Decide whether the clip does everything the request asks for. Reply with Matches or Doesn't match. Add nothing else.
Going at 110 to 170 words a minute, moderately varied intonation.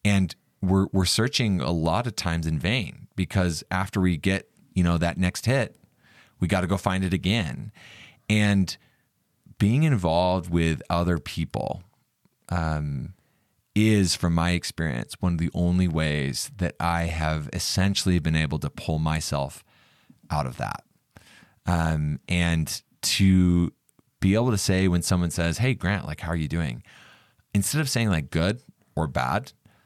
Matches